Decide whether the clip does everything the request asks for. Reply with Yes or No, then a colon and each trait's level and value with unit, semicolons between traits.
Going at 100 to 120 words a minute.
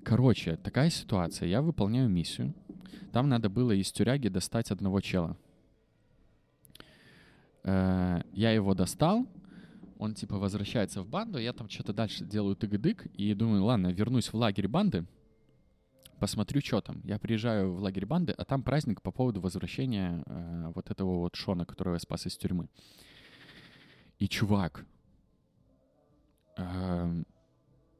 No: average, 130 wpm